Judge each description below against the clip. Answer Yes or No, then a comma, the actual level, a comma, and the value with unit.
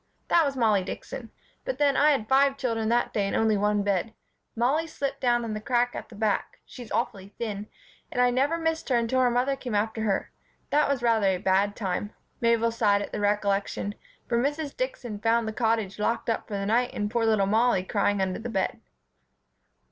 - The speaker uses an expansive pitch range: No, average, 3.4 semitones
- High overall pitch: Yes, high, 230 Hz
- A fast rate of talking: Yes, fast, 210 wpm